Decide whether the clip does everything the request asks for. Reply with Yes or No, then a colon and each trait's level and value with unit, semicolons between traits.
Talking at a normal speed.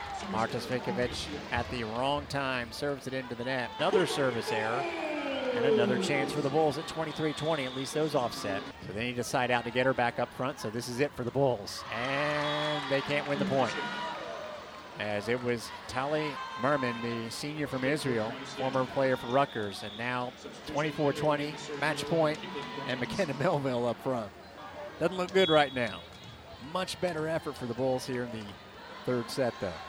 Yes: average, 185 wpm